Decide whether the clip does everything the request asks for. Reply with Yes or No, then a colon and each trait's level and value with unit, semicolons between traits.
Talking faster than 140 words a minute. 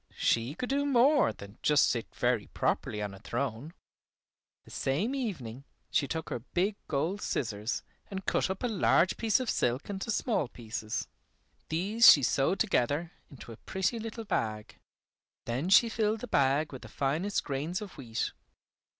Yes: average, 165 wpm